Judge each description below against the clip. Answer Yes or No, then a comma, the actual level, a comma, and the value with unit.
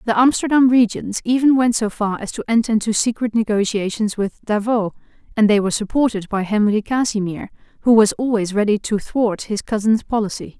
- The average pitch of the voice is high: Yes, high, 220 Hz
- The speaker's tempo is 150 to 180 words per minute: Yes, average, 175 wpm